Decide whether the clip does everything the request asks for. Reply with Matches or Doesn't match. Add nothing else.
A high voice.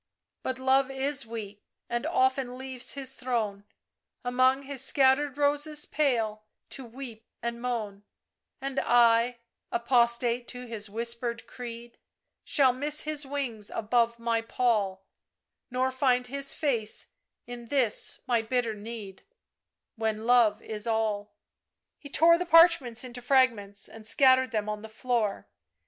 Matches